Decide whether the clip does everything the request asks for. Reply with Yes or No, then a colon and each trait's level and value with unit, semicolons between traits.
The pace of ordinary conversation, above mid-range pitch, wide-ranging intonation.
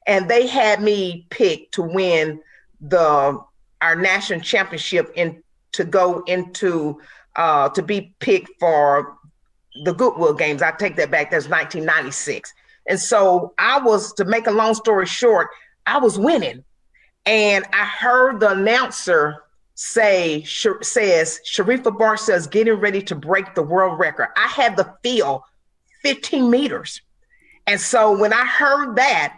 Yes: average, 145 wpm; high, 205 Hz; wide, 5.7 semitones